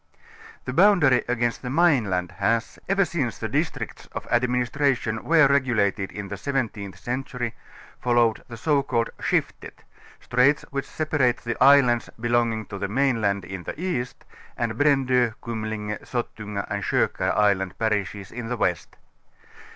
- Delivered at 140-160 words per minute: Yes, average, 145 wpm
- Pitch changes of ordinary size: Yes, average, 4.0 semitones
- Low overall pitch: Yes, low, 120 Hz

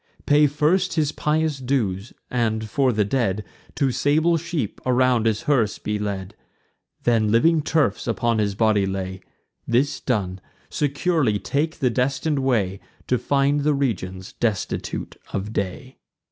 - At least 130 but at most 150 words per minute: Yes, average, 140 wpm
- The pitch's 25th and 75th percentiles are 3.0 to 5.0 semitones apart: No, wide, 5.6 semitones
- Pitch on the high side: No, low, 125 Hz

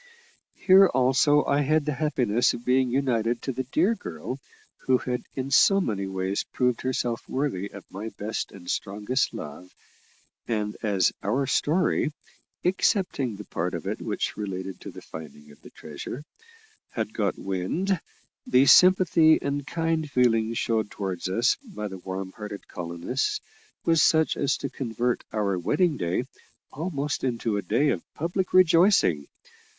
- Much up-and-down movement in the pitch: Yes, wide, 6.8 semitones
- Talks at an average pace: Yes, average, 155 wpm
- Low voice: Yes, low, 125 Hz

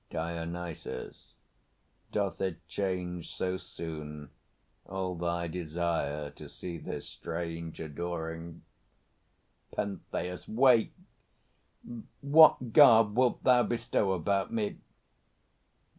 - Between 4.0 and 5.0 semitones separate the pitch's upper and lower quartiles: No, average, 3.6 semitones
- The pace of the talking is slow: Yes, slow, 85 wpm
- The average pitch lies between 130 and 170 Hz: No, very low, 90 Hz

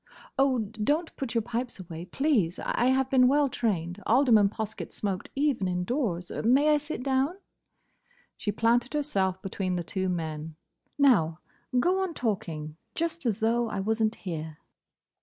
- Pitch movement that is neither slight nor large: No, wide, 6.4 semitones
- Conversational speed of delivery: Yes, average, 150 wpm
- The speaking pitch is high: Yes, high, 225 Hz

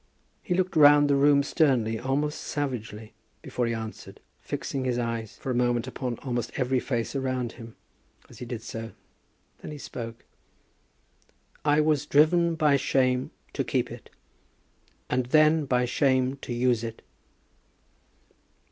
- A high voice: No, low, 130 Hz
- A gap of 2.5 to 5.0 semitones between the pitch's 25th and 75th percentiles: Yes, average, 3.4 semitones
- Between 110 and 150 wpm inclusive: Yes, average, 145 wpm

